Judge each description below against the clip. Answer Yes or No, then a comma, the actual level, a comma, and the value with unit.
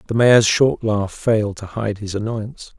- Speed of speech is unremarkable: Yes, average, 195 wpm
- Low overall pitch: Yes, low, 110 Hz